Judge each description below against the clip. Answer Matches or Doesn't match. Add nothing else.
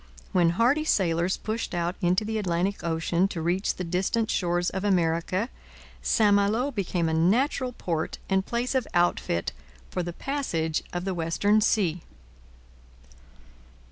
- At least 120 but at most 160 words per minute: Matches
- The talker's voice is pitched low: Doesn't match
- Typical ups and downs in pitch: Matches